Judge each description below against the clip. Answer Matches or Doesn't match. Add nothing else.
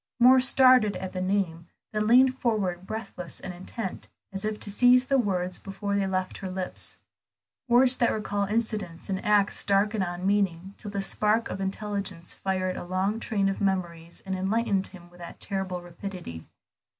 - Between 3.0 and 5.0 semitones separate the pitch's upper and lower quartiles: Doesn't match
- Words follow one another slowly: Doesn't match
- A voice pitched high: Matches